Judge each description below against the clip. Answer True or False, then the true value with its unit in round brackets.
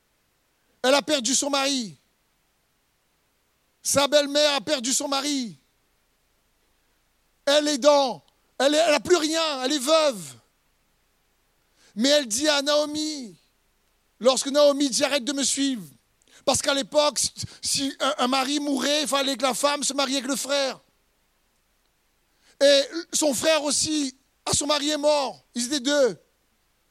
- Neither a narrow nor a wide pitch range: False (1.7 semitones)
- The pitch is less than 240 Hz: False (285 Hz)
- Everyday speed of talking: False (140 wpm)